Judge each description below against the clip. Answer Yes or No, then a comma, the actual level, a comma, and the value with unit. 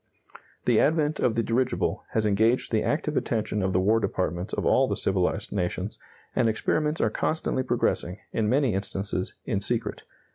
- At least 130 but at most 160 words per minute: No, average, 170 wpm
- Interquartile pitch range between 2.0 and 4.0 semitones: No, average, 4.6 semitones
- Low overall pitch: Yes, low, 110 Hz